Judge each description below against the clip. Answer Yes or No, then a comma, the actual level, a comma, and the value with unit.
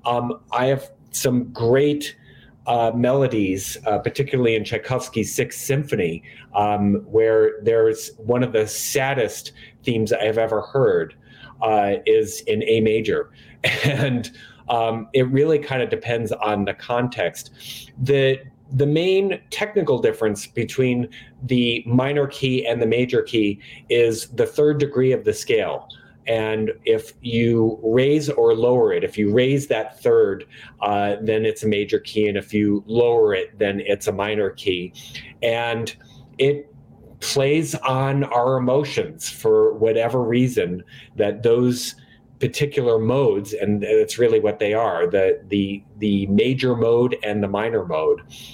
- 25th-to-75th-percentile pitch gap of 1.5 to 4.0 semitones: No, average, 4.5 semitones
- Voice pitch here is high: No, low, 125 Hz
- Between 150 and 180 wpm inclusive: No, average, 140 wpm